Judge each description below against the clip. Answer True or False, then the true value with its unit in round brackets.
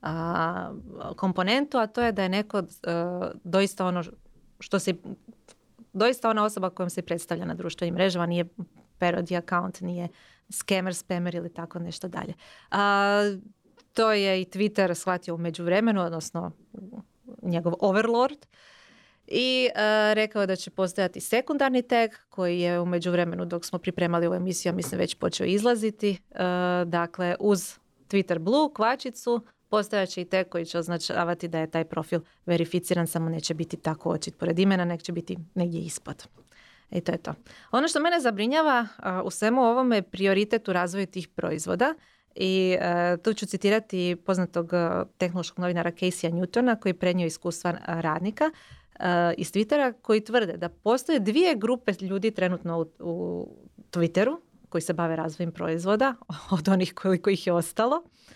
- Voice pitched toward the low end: False (185 Hz)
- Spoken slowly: False (155 wpm)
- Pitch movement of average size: True (3.6 semitones)